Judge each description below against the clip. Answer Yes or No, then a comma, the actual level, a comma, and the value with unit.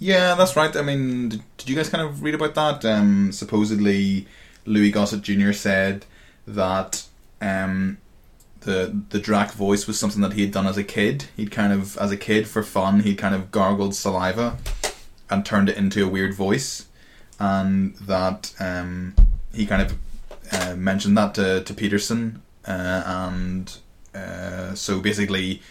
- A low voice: Yes, low, 100 Hz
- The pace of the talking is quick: No, average, 165 wpm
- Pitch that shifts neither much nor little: No, narrow, 1.8 semitones